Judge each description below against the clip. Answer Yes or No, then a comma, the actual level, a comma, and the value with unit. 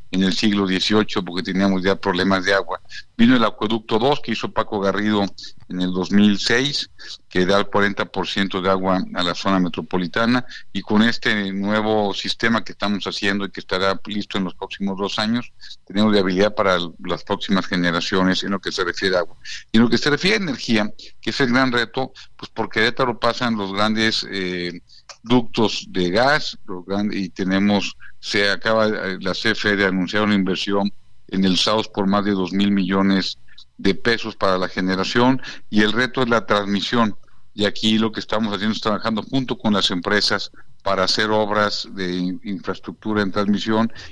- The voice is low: Yes, low, 100 Hz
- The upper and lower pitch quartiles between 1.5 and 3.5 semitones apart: Yes, narrow, 2.4 semitones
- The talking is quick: No, average, 180 wpm